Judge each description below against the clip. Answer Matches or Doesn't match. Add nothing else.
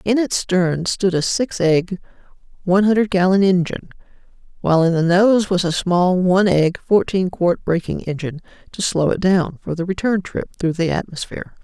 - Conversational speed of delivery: Matches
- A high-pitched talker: Doesn't match